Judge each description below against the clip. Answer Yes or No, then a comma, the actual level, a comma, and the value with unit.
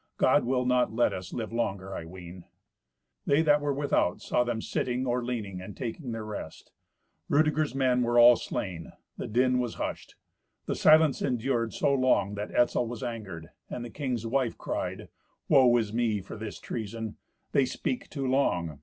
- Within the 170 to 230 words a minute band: Yes, average, 175 wpm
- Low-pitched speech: Yes, low, 120 Hz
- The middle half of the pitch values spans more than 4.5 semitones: No, average, 3.5 semitones